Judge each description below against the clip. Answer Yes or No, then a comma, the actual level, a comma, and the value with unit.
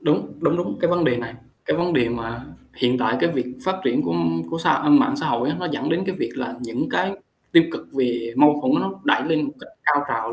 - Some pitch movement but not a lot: No, wide, 6.6 semitones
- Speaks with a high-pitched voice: No, medium, 145 Hz